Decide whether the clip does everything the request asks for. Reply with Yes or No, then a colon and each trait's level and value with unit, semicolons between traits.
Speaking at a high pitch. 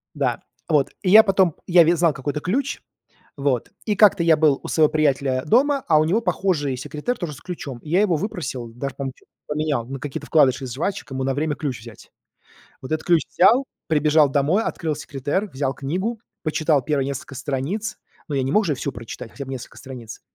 No: medium, 150 Hz